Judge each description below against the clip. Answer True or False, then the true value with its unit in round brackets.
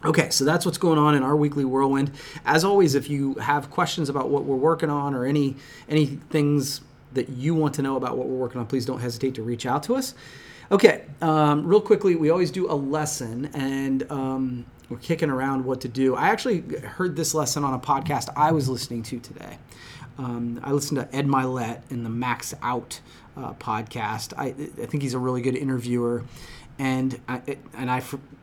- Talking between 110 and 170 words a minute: False (205 wpm)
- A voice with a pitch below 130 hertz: False (140 Hz)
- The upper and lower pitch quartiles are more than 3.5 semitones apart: False (2.8 semitones)